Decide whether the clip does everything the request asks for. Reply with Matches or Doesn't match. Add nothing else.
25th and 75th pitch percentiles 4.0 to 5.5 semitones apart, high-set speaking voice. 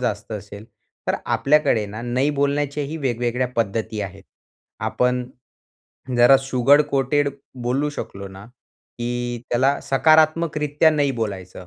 Doesn't match